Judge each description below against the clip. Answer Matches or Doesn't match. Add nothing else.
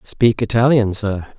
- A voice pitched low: Matches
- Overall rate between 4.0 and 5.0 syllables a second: Matches